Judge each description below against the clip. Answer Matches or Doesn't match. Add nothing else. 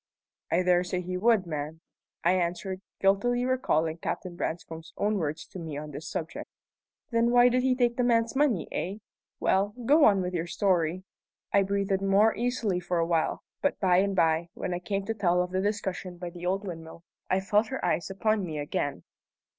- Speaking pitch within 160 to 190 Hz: Matches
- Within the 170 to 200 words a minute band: Matches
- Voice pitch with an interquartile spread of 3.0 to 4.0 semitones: Matches